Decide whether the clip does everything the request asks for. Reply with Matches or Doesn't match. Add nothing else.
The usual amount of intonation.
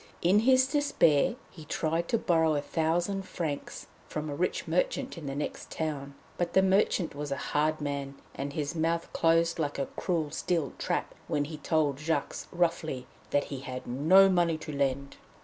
Matches